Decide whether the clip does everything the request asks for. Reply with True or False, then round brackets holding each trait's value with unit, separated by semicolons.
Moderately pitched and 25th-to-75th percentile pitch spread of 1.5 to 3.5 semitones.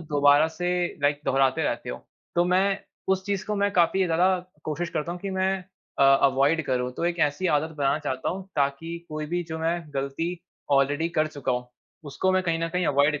False (160 Hz; 4.0 semitones)